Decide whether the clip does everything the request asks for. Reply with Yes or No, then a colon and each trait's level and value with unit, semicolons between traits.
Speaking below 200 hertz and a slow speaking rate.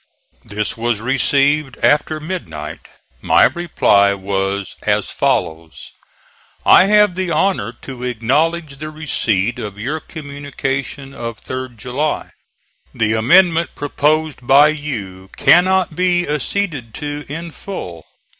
Yes: medium, 140 Hz; slow, 115 wpm